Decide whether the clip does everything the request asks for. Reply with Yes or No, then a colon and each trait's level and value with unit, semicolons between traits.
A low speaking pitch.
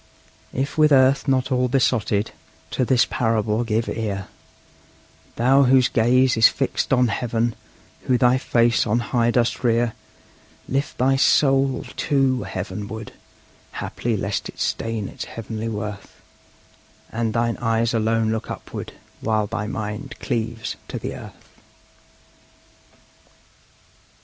Yes: low, 115 Hz